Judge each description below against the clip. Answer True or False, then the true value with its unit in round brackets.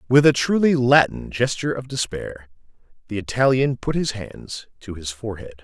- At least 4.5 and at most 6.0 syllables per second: True (5.1 syllables/s)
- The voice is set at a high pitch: False (120 Hz)